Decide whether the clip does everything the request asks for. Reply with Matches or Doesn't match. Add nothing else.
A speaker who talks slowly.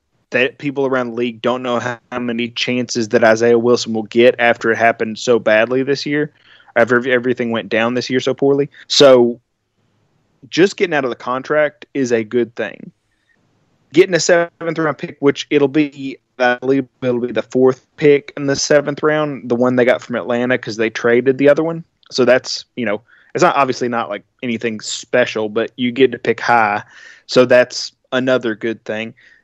Doesn't match